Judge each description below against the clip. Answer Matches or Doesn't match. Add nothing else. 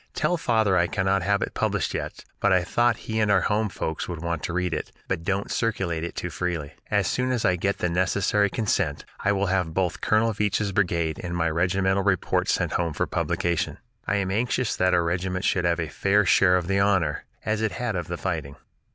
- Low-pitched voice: Matches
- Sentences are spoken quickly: Matches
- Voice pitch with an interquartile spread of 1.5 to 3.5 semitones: Matches